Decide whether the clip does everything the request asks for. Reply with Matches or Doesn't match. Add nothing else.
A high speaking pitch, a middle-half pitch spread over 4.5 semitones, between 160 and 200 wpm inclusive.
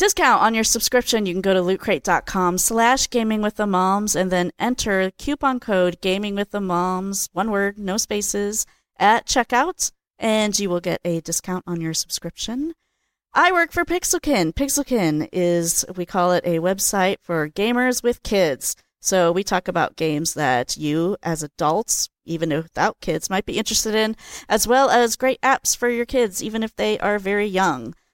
Matches